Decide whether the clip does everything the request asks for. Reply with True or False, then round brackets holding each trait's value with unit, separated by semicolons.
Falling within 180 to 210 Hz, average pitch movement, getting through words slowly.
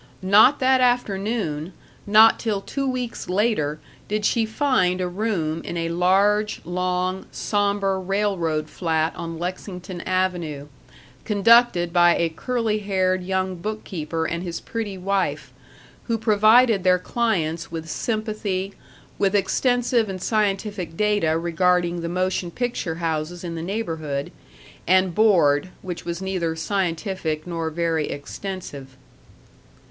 True (185 Hz; 3.9 semitones; 125 wpm)